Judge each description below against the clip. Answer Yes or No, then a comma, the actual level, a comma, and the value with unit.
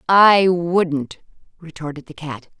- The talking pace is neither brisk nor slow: No, slow, 115 wpm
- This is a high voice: No, medium, 165 Hz